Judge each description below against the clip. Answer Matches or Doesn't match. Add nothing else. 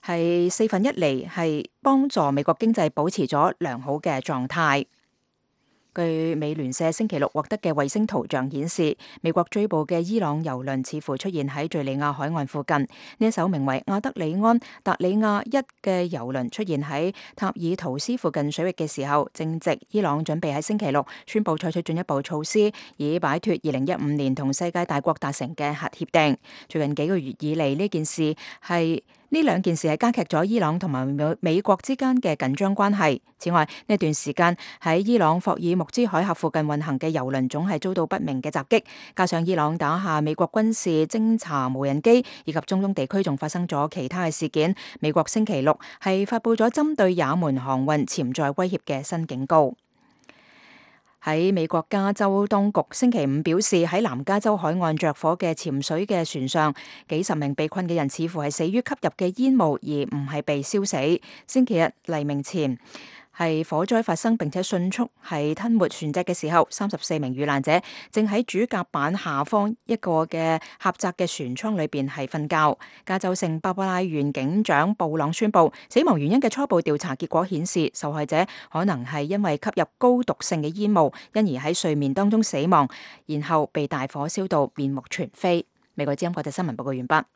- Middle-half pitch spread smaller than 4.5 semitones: Doesn't match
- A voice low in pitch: Doesn't match